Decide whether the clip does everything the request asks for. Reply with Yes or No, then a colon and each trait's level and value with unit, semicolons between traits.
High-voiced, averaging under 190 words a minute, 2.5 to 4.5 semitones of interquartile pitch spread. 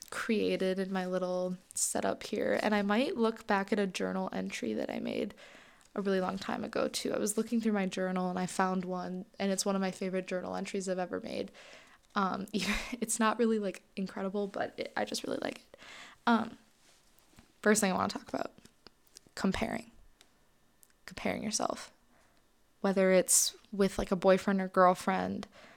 Yes: high, 195 Hz; average, 180 wpm; average, 2.8 semitones